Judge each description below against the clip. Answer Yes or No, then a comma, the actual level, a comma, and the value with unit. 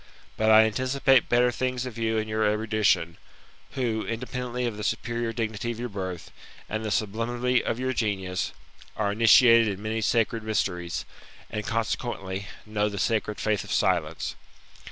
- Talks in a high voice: No, low, 110 Hz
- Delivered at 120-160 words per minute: Yes, average, 155 wpm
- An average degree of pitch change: No, narrow, 2.2 semitones